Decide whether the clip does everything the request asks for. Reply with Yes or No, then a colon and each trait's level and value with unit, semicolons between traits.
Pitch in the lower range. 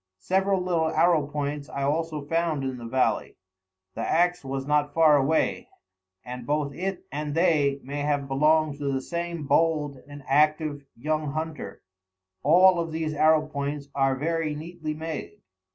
No: medium, 150 Hz